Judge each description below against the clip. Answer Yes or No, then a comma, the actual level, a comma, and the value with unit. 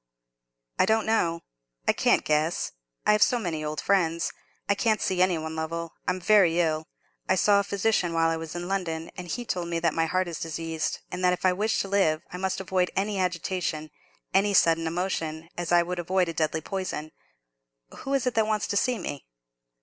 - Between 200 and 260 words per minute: Yes, fast, 205 wpm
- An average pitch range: Yes, average, 3.2 semitones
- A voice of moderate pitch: Yes, medium, 175 Hz